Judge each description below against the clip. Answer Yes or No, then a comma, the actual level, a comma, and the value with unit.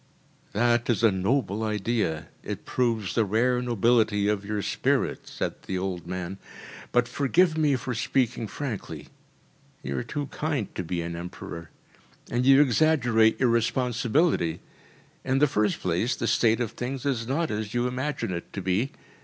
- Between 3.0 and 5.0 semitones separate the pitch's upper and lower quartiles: Yes, average, 4.5 semitones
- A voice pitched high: No, low, 115 Hz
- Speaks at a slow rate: No, average, 160 wpm